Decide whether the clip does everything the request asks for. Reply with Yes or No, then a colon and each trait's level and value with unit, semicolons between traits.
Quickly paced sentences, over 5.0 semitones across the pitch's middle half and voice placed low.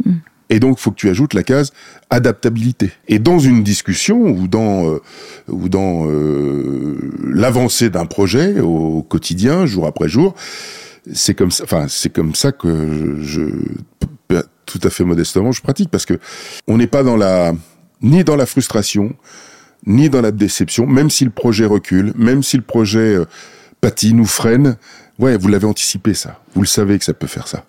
No: average, 180 wpm; wide, 5.6 semitones; low, 110 Hz